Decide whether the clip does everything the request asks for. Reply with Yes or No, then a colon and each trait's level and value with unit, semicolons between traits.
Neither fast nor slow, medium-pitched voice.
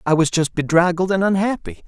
Yes: average, 190 wpm; medium, 175 Hz